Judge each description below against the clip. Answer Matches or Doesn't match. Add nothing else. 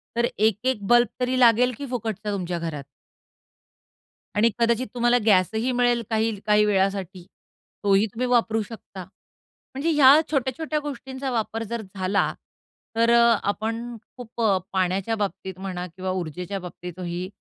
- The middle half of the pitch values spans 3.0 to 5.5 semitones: Matches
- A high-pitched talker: Matches